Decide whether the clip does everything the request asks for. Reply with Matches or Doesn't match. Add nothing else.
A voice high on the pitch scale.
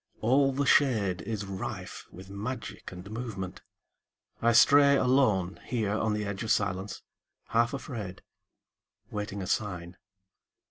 Doesn't match